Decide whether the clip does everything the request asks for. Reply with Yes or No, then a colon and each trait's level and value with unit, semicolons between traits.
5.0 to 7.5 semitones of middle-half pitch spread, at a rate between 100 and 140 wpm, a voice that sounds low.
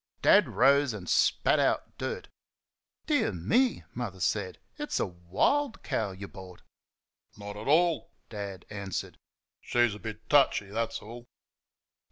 Yes: wide, 5.4 semitones; slow, 135 wpm; low, 105 Hz